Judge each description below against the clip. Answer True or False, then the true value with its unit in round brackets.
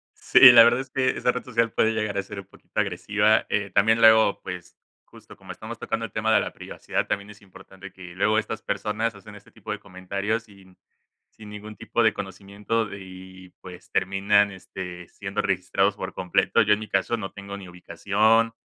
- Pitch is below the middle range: True (100 Hz)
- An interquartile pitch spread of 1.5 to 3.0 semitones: True (2.5 semitones)